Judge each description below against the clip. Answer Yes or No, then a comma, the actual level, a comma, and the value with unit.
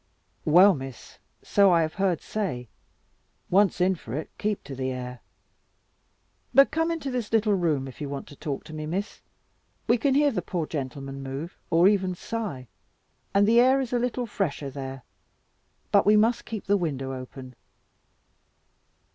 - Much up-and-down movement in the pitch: Yes, wide, 7.6 semitones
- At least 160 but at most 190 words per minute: Yes, average, 170 wpm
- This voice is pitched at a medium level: Yes, medium, 175 Hz